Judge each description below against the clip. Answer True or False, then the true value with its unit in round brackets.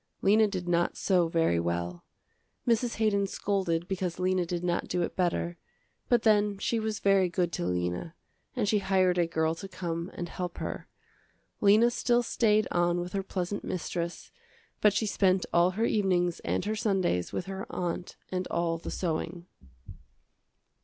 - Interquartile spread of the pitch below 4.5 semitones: True (2.8 semitones)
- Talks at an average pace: True (165 wpm)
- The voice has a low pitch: False (180 Hz)